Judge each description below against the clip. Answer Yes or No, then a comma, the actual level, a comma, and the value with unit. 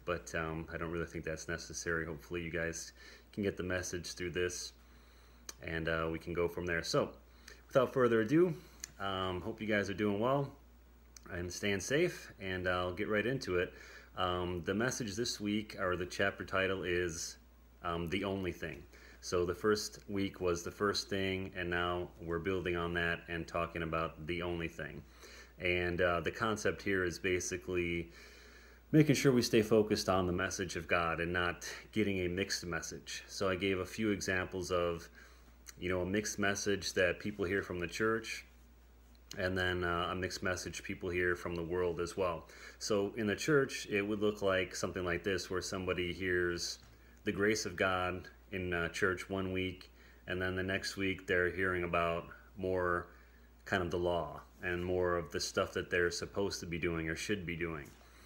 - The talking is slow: No, average, 185 wpm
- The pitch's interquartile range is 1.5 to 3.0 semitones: Yes, narrow, 2.5 semitones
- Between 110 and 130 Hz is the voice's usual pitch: No, very low, 90 Hz